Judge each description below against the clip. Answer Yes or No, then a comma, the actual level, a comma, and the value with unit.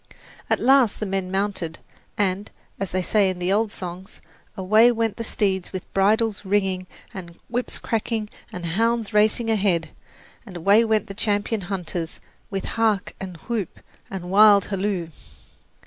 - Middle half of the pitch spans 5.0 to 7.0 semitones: No, average, 2.8 semitones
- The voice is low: No, high, 200 Hz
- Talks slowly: No, average, 150 wpm